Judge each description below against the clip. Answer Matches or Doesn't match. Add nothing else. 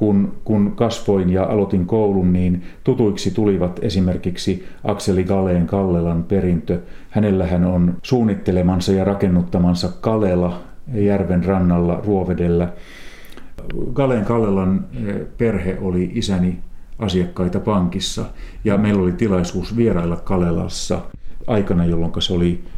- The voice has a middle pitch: Doesn't match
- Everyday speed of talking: Matches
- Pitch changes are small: Matches